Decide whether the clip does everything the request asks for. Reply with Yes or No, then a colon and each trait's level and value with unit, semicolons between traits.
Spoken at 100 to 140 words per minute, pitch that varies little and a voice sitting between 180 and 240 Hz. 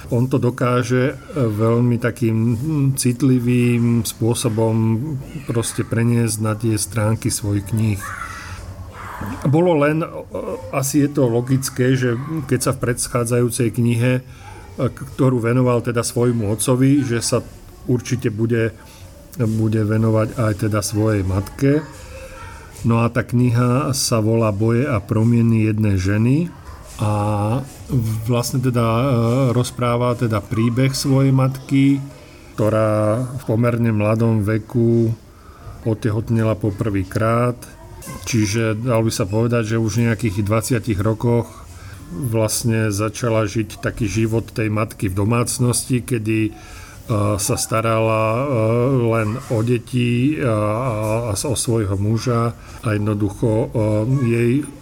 No: slow, 110 wpm; narrow, 2.3 semitones; low, 115 Hz